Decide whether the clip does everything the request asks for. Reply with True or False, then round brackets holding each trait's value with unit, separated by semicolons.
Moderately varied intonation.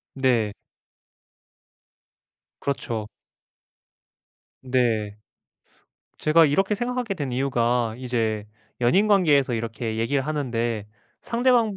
False (6.1 semitones)